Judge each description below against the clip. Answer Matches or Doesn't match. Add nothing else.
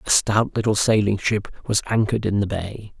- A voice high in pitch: Doesn't match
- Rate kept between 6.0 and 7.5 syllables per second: Doesn't match